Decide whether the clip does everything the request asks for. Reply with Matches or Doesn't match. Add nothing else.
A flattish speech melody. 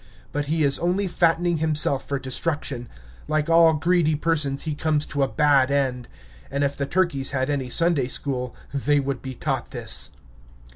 Doesn't match